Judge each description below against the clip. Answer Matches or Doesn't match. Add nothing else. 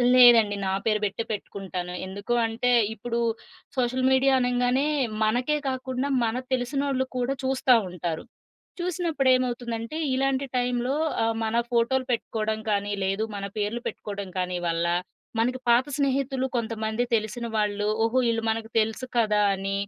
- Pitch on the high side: Matches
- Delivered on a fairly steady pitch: Doesn't match